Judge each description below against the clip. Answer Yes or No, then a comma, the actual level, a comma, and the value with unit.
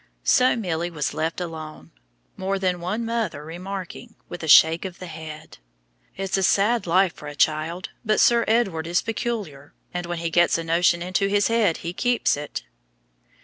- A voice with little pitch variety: No, average, 3.7 semitones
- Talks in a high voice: No, medium, 175 Hz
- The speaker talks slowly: No, average, 185 wpm